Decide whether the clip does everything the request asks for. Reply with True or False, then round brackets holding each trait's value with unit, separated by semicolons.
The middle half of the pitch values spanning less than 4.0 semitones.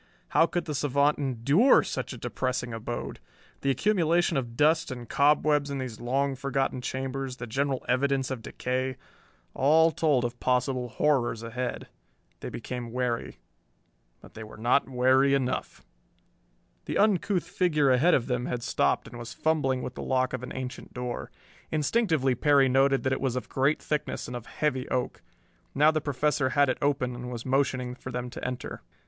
True (2.7 semitones)